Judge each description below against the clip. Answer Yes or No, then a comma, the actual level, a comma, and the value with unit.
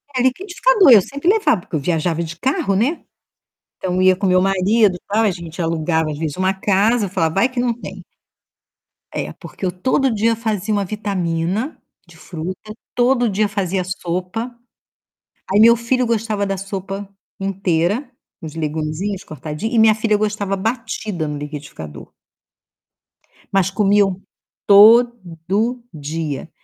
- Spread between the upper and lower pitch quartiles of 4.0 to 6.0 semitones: Yes, average, 4.4 semitones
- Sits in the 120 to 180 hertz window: No, high, 195 Hz